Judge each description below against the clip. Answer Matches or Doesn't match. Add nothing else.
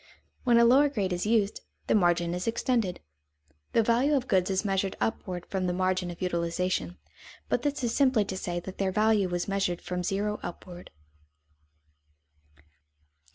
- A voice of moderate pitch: Doesn't match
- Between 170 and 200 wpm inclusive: Doesn't match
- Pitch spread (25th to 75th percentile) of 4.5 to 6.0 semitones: Doesn't match